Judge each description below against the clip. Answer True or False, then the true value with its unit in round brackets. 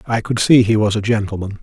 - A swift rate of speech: True (260 wpm)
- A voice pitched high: False (110 Hz)